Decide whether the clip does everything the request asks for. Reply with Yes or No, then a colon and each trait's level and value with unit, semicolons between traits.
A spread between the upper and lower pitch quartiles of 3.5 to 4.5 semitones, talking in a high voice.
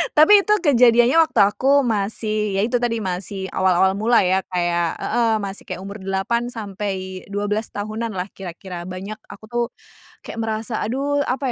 Yes: average, 3.8 semitones; high, 210 Hz